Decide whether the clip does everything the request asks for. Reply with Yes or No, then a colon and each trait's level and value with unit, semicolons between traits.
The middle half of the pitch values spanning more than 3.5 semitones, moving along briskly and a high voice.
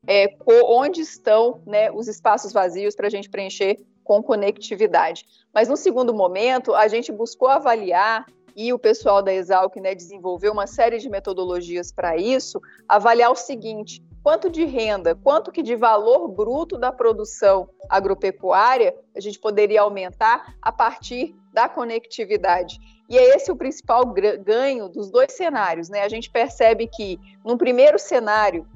No: average, 4.1 semitones; average, 155 wpm; high, 220 Hz